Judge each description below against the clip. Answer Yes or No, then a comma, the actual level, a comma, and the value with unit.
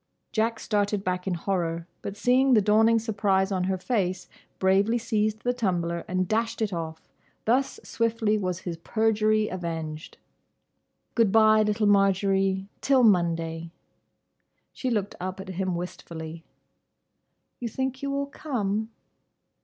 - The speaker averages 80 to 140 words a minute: Yes, slow, 135 wpm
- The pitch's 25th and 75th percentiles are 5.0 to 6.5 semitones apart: No, average, 3.5 semitones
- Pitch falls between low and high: No, high, 200 Hz